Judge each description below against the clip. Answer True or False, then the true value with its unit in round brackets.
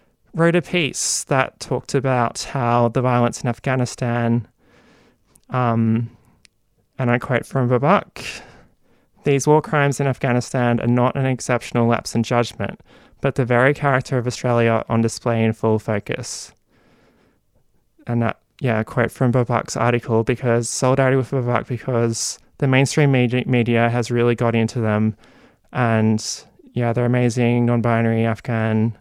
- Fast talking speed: False (140 wpm)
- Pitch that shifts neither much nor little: False (1.9 semitones)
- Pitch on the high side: False (120 Hz)